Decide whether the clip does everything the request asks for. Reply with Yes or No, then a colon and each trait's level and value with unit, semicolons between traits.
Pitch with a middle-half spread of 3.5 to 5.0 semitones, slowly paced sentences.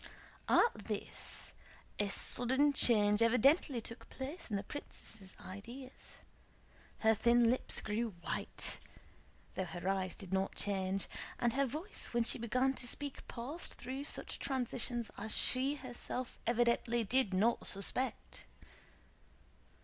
Yes: average, 4.2 semitones; slow, 125 wpm